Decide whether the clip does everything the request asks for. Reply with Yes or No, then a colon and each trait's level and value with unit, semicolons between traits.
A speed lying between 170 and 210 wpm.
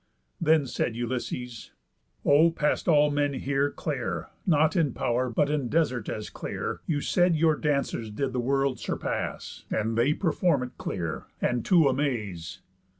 No: average, 150 wpm